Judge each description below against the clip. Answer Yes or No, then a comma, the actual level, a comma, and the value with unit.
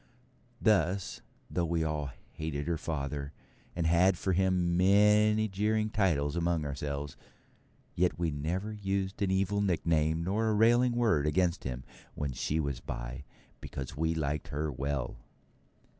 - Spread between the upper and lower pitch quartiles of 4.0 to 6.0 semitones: Yes, average, 5.1 semitones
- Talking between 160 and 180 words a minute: No, average, 145 wpm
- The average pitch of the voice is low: Yes, very low, 85 Hz